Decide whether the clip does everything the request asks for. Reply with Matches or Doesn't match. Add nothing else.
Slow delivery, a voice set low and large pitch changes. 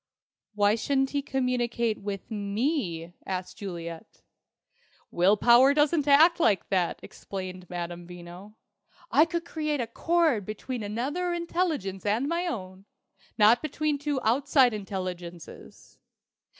Doesn't match